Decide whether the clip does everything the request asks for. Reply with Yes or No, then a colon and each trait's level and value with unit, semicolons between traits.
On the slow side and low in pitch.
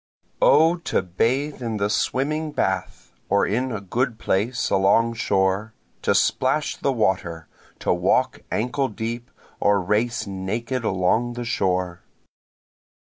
Yes: slow, 130 wpm; low, 115 Hz